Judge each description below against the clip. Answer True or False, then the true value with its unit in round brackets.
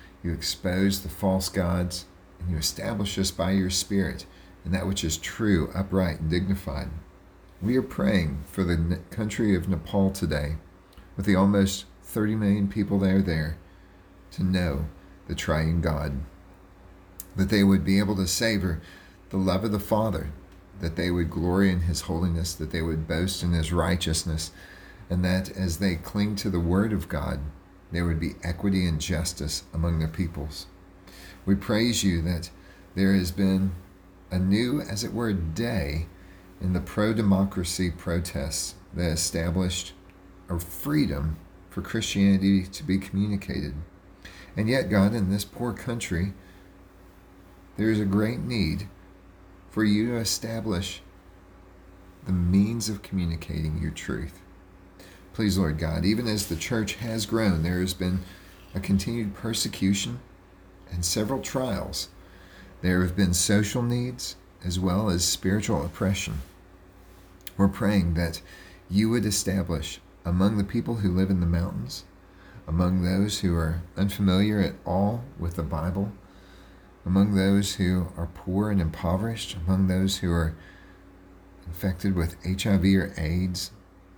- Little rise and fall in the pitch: True (1.7 semitones)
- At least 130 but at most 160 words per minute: True (145 wpm)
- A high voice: False (95 Hz)